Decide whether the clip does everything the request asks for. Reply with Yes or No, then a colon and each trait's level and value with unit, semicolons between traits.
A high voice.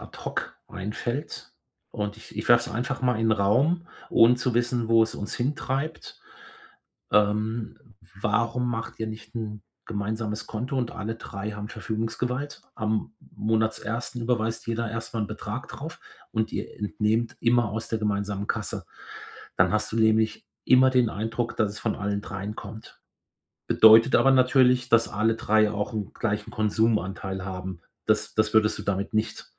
No: low, 110 Hz